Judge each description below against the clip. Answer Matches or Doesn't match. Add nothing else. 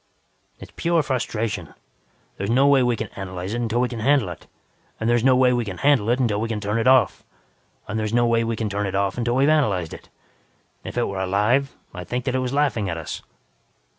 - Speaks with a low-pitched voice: Matches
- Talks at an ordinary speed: Doesn't match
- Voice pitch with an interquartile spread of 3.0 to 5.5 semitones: Matches